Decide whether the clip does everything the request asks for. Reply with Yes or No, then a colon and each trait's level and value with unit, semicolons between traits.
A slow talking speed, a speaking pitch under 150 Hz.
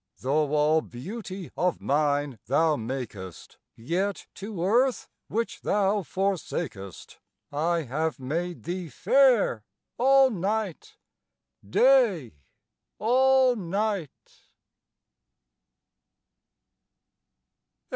No: slow, 75 wpm; medium, 175 Hz